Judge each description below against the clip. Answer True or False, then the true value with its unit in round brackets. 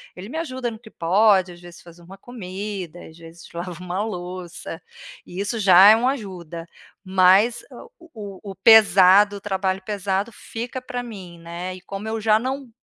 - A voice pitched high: True (195 Hz)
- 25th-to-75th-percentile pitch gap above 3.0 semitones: True (3.7 semitones)